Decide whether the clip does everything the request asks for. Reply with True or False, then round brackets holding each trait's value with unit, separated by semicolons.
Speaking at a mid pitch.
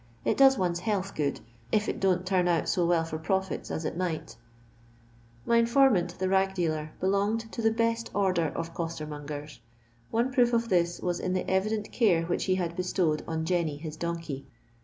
True (180 Hz)